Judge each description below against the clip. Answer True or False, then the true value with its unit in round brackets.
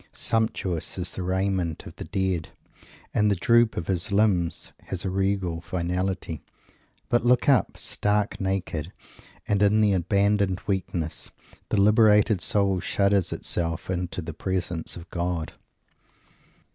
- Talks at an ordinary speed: False (130 wpm)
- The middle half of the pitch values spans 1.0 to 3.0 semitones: True (2.7 semitones)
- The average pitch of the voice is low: True (95 Hz)